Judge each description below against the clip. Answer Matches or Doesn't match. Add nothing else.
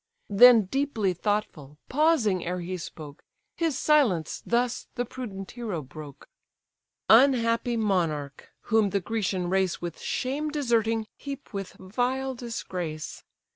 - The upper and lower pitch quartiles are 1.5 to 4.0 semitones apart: Doesn't match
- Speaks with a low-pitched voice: Doesn't match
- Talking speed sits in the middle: Doesn't match